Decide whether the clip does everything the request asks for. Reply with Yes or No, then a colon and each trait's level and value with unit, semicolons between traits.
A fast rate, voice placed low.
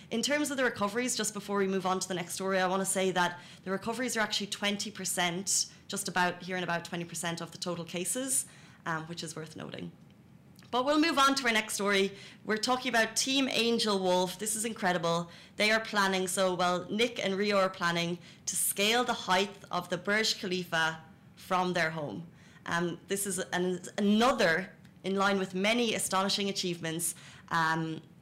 No: fast, 190 wpm; high, 190 Hz